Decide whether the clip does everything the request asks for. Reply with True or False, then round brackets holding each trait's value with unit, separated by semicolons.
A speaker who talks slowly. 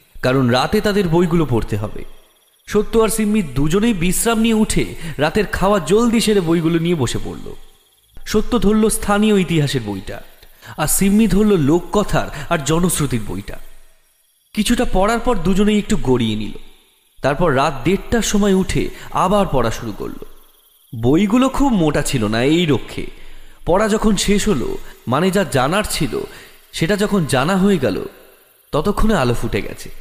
False (145 wpm)